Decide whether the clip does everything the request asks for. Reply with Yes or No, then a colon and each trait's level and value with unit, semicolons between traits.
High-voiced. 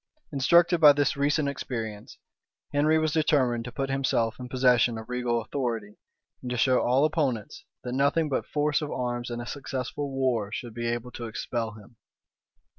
No: low, 125 Hz